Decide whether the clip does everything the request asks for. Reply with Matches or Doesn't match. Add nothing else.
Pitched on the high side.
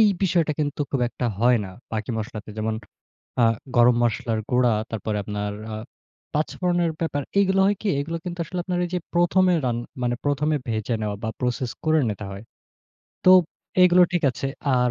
Doesn't match